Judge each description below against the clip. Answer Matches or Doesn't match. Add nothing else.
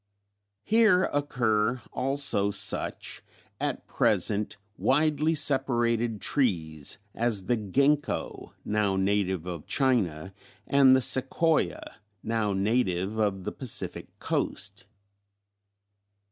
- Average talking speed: Doesn't match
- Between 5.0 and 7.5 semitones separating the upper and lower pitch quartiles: Matches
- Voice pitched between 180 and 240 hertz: Doesn't match